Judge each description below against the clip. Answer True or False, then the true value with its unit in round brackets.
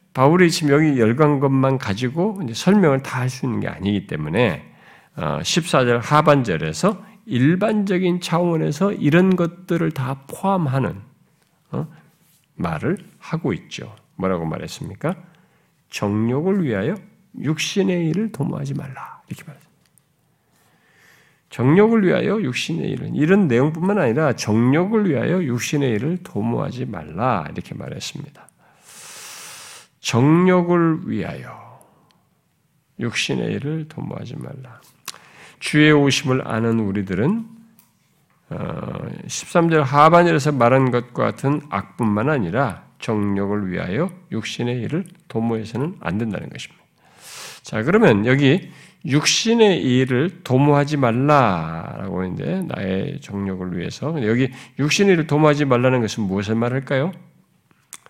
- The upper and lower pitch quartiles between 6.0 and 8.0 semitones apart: False (5.5 semitones)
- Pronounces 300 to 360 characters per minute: False (270 characters per minute)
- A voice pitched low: False (150 Hz)